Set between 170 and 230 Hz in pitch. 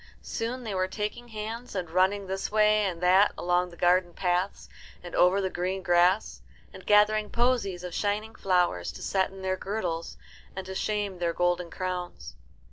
Yes: high, 190 Hz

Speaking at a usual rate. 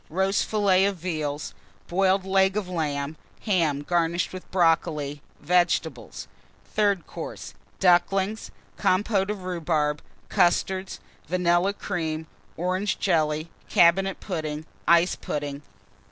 No: slow, 105 wpm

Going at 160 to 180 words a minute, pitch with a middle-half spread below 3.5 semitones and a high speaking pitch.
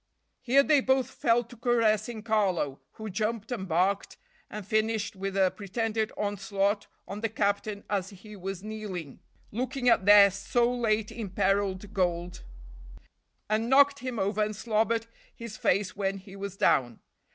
No: average, 150 wpm; average, 2.7 semitones; high, 210 Hz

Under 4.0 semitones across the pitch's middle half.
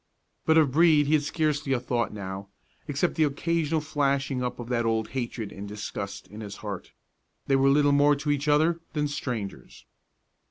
No: average, 4.7 semitones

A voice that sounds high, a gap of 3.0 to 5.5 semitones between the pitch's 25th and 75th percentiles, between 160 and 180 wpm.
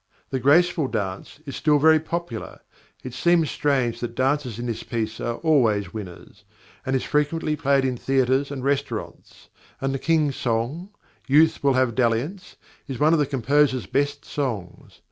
No: low, 135 Hz; average, 3.9 semitones; average, 165 wpm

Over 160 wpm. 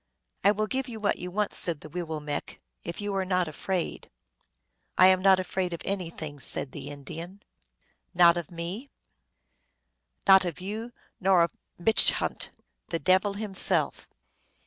Yes: average, 180 wpm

